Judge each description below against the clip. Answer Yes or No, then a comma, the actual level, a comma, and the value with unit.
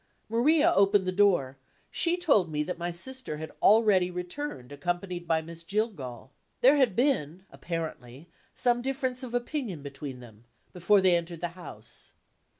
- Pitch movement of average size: No, wide, 7.1 semitones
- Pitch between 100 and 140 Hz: No, medium, 180 Hz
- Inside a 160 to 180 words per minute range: No, average, 150 wpm